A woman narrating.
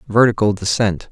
No: male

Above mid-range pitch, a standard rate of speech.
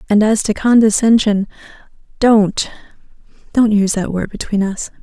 No: high, 210 Hz; slow, 120 wpm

